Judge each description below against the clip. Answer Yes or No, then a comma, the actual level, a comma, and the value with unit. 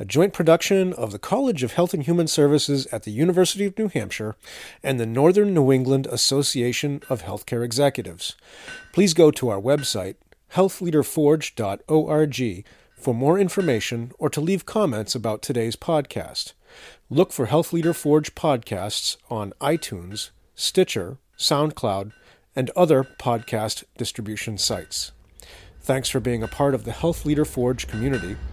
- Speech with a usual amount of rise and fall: No, wide, 5.8 semitones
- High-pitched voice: No, low, 135 Hz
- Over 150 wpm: No, average, 145 wpm